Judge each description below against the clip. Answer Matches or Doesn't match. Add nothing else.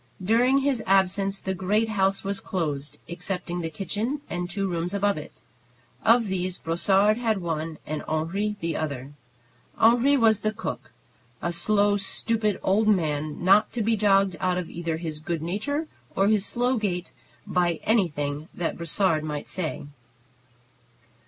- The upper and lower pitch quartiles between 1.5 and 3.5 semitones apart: Doesn't match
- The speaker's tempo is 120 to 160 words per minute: Matches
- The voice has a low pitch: Doesn't match